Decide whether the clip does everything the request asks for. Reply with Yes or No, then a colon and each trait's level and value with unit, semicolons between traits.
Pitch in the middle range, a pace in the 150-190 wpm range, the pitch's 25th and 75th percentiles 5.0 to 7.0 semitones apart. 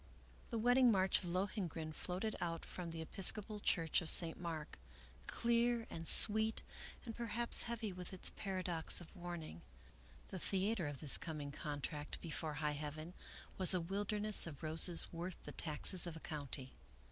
No: medium, 175 Hz; average, 160 wpm; average, 4.5 semitones